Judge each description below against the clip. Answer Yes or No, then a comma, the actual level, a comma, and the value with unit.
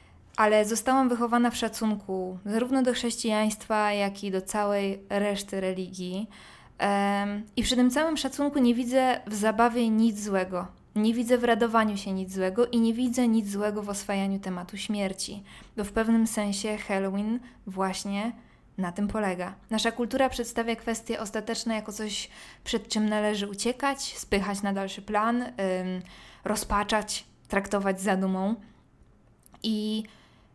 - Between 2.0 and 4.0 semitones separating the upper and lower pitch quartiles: Yes, narrow, 2.5 semitones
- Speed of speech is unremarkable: Yes, average, 140 wpm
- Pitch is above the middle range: Yes, high, 215 Hz